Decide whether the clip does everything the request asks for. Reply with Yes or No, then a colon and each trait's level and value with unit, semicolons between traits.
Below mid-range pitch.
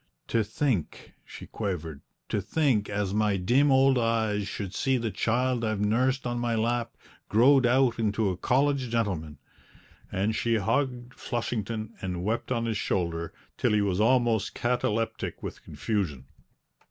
Yes: low, 115 Hz